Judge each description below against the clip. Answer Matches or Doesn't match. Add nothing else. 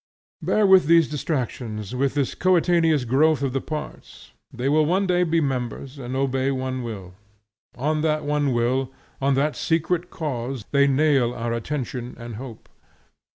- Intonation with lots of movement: Doesn't match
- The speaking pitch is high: Doesn't match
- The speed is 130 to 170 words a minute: Matches